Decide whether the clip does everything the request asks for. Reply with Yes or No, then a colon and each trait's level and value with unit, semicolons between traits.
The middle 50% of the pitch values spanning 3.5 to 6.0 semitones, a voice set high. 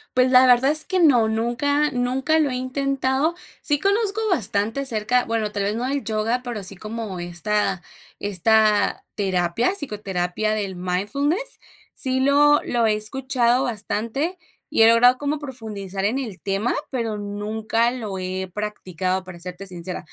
Yes: average, 4.7 semitones; high, 225 Hz